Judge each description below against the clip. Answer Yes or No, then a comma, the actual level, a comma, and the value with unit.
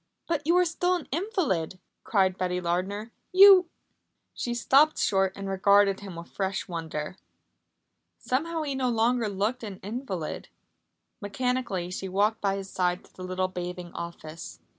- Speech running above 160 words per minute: No, average, 155 wpm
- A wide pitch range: Yes, wide, 5.8 semitones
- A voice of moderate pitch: No, high, 200 Hz